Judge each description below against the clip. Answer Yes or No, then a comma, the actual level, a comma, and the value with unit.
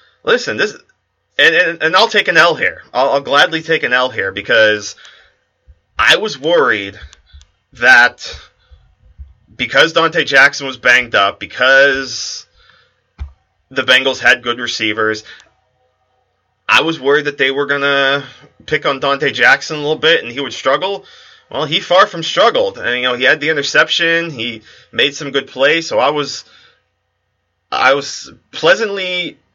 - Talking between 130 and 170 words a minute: Yes, average, 150 wpm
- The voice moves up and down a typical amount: No, wide, 7.6 semitones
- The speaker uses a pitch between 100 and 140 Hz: Yes, low, 135 Hz